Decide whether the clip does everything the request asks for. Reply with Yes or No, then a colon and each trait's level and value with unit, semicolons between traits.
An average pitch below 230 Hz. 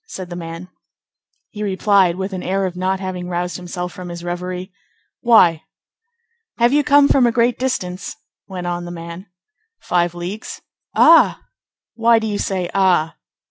Yes: medium, 185 Hz